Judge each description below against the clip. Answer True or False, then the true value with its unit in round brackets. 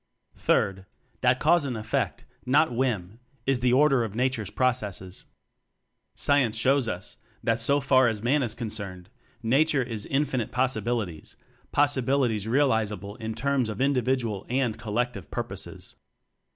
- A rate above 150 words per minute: False (140 wpm)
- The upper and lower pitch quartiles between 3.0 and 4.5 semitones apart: True (3.6 semitones)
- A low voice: True (120 Hz)